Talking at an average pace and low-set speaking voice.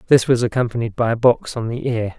No: fast, 245 wpm; low, 120 Hz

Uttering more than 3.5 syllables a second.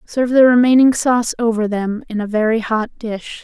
Yes: 5.2 syllables/s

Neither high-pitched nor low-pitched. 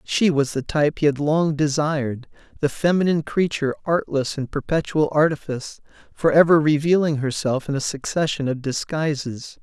Yes: medium, 150 Hz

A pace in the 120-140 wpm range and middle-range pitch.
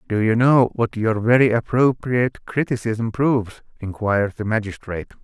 No: slow, 135 wpm; low, 115 Hz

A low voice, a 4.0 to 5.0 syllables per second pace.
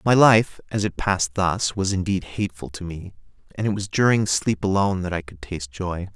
No: very low, 95 Hz; 5.5 syllables/s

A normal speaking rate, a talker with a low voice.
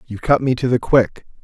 No: fast, 250 wpm; low, 125 Hz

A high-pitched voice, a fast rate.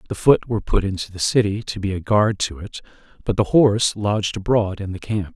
No: low, 105 Hz; fast, 235 wpm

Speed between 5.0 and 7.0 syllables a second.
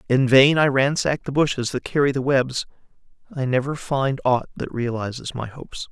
Yes: 5.2 syllables/s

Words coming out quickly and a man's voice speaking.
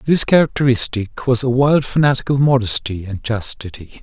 No: slow, 135 wpm; male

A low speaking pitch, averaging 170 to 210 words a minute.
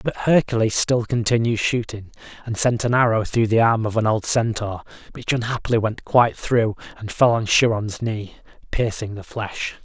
Yes: low, 115 Hz; average, 175 wpm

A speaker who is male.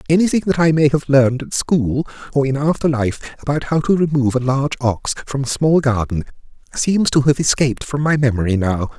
Yes: male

